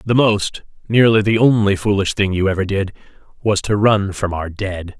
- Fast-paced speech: No, average, 180 wpm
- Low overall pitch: Yes, low, 100 Hz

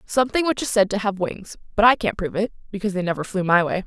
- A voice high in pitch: Yes, high, 205 Hz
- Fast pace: Yes, fast, 280 wpm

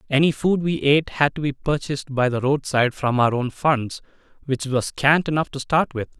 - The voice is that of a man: Yes, male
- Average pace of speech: No, fast, 215 wpm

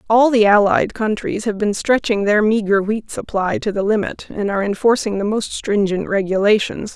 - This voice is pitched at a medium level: No, high, 210 Hz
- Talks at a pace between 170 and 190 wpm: Yes, average, 180 wpm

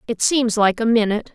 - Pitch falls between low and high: No, high, 225 Hz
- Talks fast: Yes, fast, 225 wpm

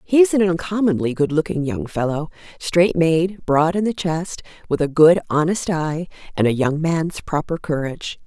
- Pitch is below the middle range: No, medium, 165 Hz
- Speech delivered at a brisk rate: No, average, 180 wpm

